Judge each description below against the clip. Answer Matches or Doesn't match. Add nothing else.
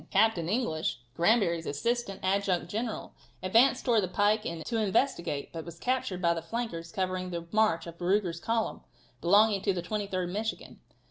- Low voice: Doesn't match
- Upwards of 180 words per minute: Doesn't match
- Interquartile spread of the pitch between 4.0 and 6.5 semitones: Matches